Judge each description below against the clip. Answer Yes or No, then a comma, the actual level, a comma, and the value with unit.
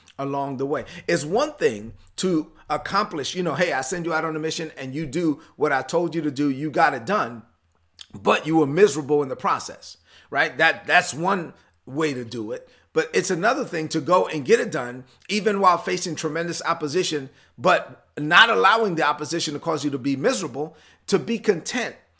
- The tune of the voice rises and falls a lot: No, average, 3.9 semitones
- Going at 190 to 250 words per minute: Yes, fast, 205 wpm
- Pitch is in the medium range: Yes, medium, 160 Hz